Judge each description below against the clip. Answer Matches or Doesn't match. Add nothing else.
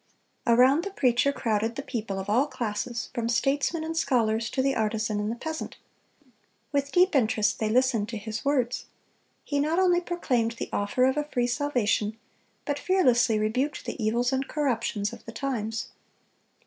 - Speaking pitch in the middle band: Doesn't match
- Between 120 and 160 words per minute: Doesn't match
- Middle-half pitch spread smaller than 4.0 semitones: Doesn't match